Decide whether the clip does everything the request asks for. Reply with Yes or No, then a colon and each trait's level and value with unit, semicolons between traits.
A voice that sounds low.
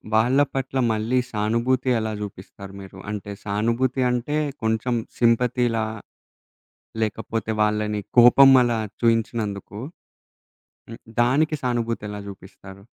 Yes: low, 115 Hz